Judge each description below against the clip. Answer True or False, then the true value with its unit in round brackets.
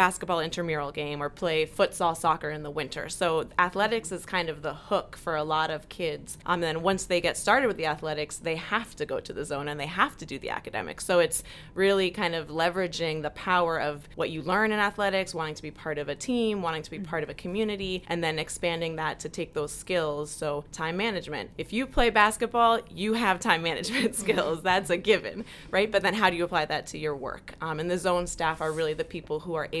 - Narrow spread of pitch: False (3.8 semitones)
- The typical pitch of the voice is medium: True (170 Hz)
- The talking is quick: True (240 wpm)